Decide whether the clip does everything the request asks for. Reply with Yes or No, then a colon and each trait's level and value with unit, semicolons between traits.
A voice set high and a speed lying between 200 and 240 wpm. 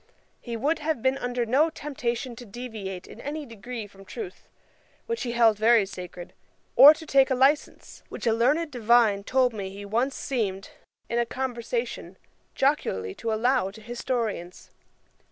No: high, 240 Hz; average, 160 wpm